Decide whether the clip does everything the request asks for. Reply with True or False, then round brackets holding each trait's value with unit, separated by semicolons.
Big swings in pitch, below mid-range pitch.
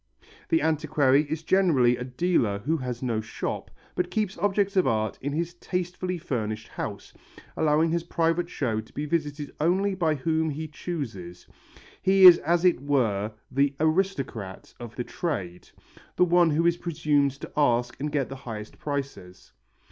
False (5.7 semitones; 150 Hz)